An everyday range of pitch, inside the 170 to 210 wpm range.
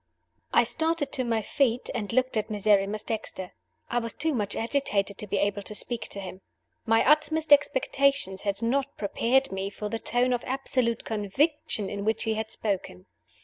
Yes: average, 4.7 semitones; average, 180 wpm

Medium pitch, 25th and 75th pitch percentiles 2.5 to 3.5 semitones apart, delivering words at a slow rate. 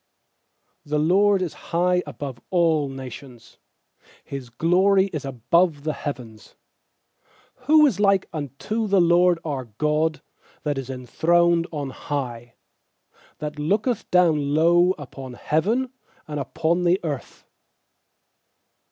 No: medium, 155 Hz; average, 4.6 semitones; slow, 115 wpm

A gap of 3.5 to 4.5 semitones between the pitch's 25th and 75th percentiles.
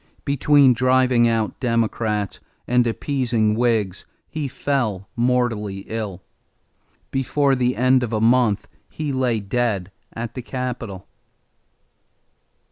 No: average, 2.9 semitones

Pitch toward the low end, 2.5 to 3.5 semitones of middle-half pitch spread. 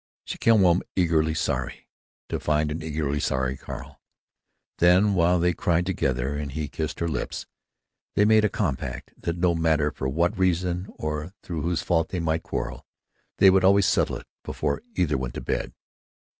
Yes: very low, 85 Hz; average, 3.2 semitones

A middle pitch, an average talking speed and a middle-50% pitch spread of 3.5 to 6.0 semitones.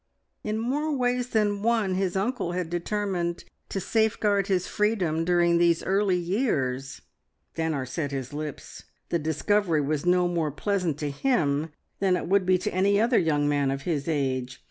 Yes: medium, 175 Hz; average, 165 wpm; average, 5.0 semitones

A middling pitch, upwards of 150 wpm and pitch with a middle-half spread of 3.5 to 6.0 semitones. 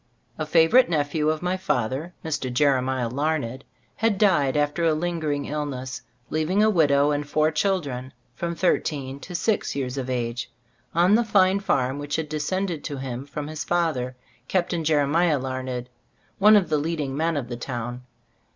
Yes: medium, 150 Hz; average, 170 wpm; average, 4.4 semitones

